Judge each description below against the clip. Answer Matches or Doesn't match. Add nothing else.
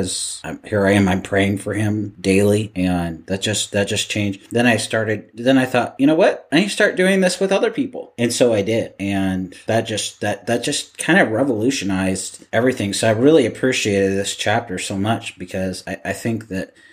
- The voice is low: Matches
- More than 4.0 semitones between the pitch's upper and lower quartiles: Doesn't match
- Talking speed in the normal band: Doesn't match